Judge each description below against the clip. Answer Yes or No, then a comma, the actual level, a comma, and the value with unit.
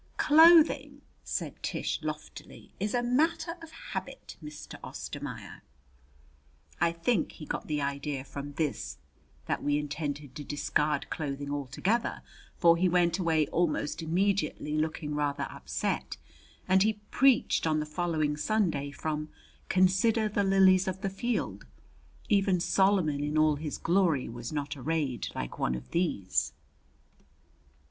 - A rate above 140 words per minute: No, slow, 135 wpm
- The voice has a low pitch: No, medium, 160 Hz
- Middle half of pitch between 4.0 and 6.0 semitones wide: Yes, average, 4.8 semitones